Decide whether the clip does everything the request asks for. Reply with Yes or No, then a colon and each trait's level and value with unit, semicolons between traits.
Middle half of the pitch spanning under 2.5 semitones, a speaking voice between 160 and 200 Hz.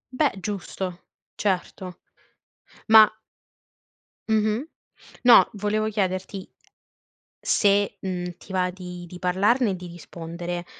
No: average, 2.8 semitones; high, 190 Hz